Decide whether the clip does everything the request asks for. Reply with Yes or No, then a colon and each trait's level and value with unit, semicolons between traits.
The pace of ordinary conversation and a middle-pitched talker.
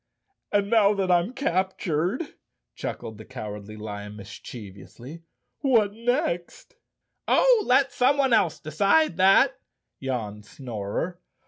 No: slow, 110 wpm; medium, 180 Hz